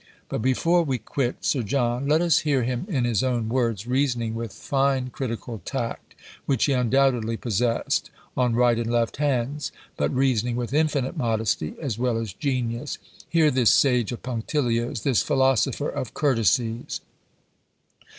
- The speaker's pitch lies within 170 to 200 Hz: No, low, 125 Hz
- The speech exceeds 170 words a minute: No, average, 150 wpm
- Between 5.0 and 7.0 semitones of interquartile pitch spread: No, average, 2.8 semitones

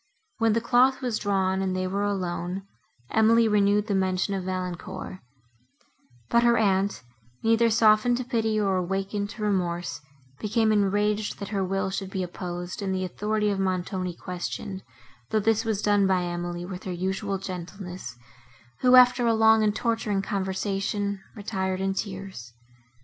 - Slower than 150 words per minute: No, average, 155 wpm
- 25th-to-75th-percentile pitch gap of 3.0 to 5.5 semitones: No, narrow, 2.6 semitones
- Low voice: No, high, 195 Hz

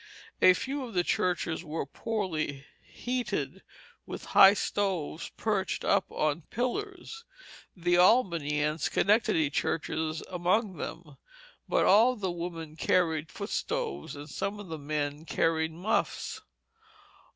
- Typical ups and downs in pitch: Yes, average, 4.9 semitones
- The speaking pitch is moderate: Yes, medium, 175 Hz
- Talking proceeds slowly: Yes, slow, 125 wpm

